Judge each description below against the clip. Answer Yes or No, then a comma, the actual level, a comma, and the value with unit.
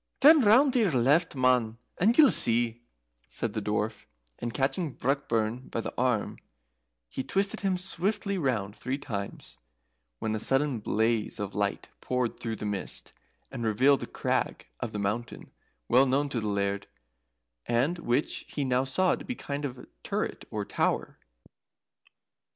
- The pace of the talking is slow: No, average, 160 wpm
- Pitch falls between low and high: No, low, 125 Hz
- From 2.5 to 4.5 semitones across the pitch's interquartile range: No, average, 4.9 semitones